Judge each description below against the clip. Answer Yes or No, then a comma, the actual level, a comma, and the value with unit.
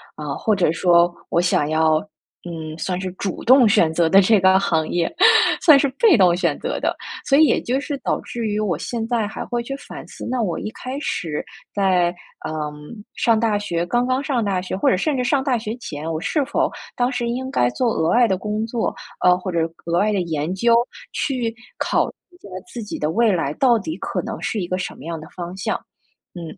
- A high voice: Yes, high, 200 Hz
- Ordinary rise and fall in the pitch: No, wide, 5.8 semitones